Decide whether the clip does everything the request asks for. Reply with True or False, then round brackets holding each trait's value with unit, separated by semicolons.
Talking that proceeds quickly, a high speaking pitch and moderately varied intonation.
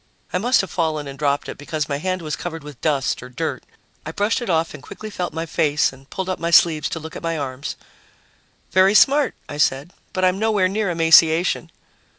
False (215 wpm; 165 Hz; 4.1 semitones)